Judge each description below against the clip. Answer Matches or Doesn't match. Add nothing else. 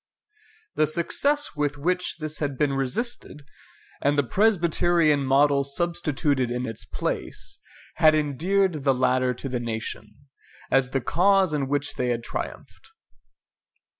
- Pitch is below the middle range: Doesn't match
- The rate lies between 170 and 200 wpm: Doesn't match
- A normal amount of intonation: Matches